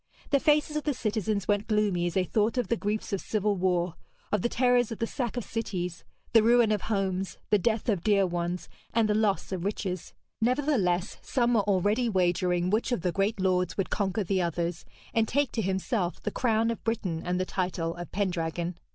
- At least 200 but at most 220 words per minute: Yes, fast, 205 wpm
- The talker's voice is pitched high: Yes, high, 205 Hz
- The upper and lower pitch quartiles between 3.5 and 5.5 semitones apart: Yes, average, 3.9 semitones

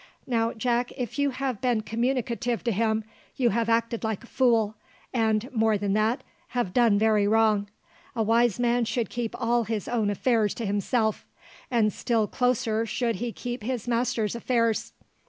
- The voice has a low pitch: No, high, 230 Hz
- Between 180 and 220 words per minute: No, average, 170 wpm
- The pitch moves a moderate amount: No, narrow, 1.9 semitones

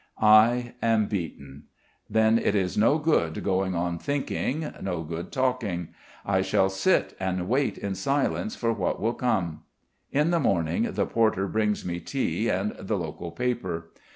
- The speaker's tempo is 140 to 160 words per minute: Yes, average, 155 wpm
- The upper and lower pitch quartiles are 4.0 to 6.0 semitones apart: Yes, wide, 5.5 semitones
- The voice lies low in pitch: Yes, low, 100 Hz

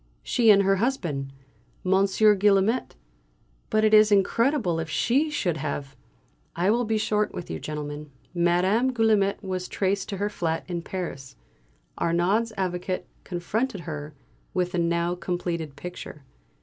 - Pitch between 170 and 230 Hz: Yes, medium, 185 Hz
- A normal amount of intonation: Yes, average, 3.9 semitones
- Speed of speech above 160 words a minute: No, average, 145 wpm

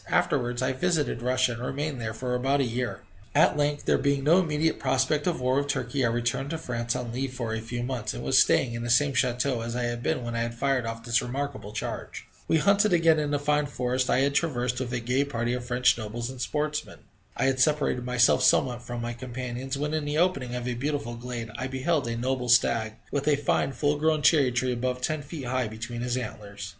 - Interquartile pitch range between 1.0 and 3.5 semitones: Yes, average, 3.1 semitones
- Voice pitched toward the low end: Yes, low, 125 Hz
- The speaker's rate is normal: No, fast, 235 wpm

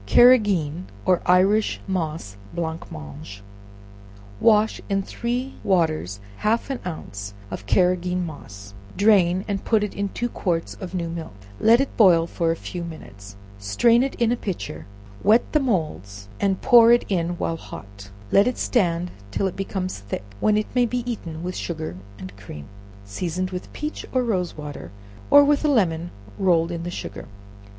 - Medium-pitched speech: Yes, medium, 180 Hz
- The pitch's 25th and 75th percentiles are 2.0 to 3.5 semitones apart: No, average, 5.2 semitones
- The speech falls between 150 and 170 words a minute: Yes, average, 165 wpm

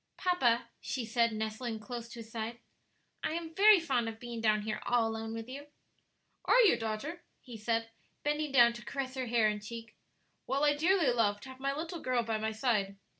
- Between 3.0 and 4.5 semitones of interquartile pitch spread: Yes, average, 3.7 semitones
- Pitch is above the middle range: Yes, high, 235 Hz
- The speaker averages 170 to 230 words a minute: Yes, fast, 205 wpm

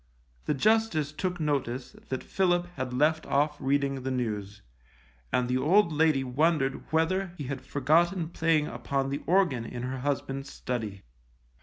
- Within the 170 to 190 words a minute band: No, average, 150 wpm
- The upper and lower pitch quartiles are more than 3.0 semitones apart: Yes, average, 3.9 semitones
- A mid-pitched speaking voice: Yes, medium, 145 Hz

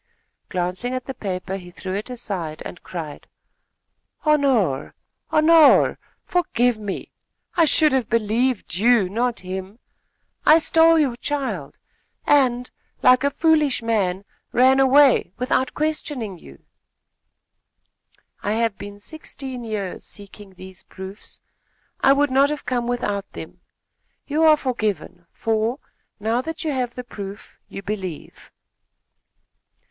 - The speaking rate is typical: No, slow, 125 wpm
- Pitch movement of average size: No, wide, 5.7 semitones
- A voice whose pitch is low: No, high, 235 Hz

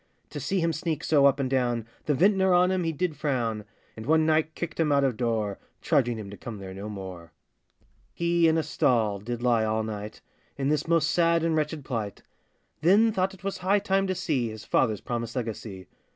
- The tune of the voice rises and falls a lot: Yes, wide, 7.2 semitones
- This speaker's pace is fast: Yes, fast, 210 wpm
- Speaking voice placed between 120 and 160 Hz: Yes, medium, 140 Hz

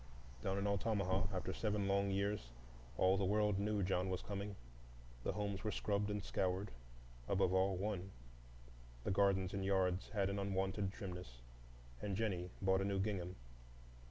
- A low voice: Yes, very low, 95 Hz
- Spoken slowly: No, average, 155 wpm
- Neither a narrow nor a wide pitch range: No, narrow, 1.5 semitones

